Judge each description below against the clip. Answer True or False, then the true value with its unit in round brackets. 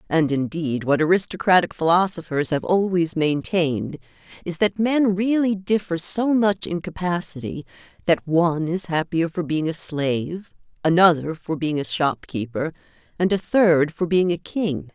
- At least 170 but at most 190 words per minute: False (150 wpm)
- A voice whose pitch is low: False (170 Hz)